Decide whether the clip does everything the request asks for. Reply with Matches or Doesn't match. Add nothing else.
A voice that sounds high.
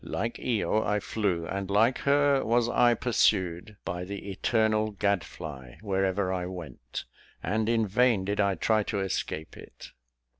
Doesn't match